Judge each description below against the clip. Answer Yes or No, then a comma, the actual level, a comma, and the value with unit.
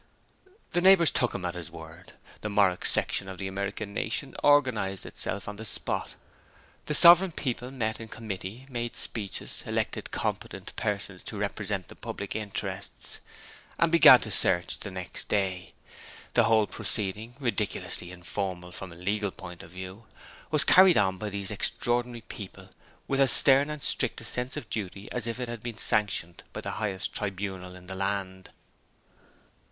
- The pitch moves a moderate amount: Yes, average, 4.1 semitones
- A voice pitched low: Yes, low, 105 Hz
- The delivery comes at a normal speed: Yes, average, 165 wpm